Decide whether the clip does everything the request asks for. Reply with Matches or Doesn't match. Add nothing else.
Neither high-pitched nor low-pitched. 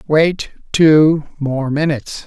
Matches